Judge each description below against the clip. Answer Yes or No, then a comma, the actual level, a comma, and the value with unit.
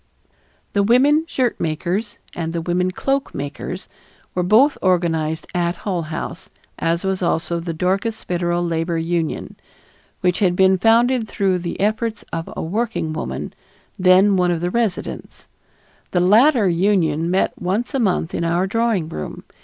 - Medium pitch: Yes, medium, 180 Hz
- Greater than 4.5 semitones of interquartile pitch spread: No, average, 3.9 semitones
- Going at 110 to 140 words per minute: No, average, 155 wpm